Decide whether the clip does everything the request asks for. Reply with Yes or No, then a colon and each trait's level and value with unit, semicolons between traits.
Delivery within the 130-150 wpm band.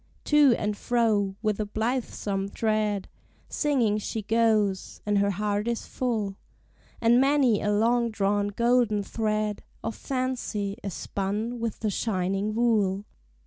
Yes: slow, 135 wpm